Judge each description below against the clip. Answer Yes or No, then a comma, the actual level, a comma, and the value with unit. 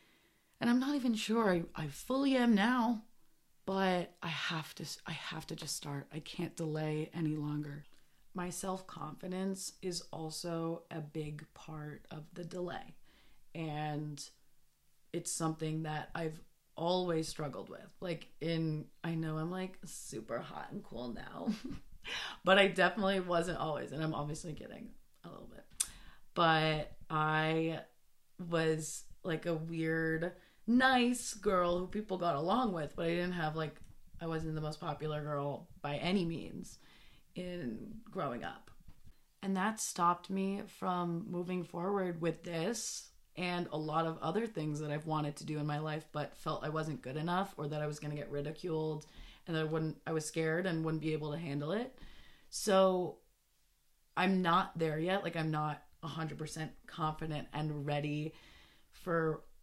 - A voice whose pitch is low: No, medium, 165 Hz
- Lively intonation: No, average, 3.0 semitones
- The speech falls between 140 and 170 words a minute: Yes, average, 160 wpm